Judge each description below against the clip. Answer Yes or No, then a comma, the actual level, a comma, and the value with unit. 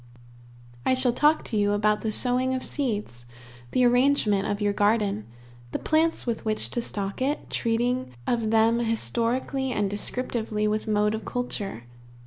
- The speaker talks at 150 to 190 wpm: Yes, average, 155 wpm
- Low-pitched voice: No, high, 225 Hz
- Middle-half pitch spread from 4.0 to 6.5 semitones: No, average, 3.2 semitones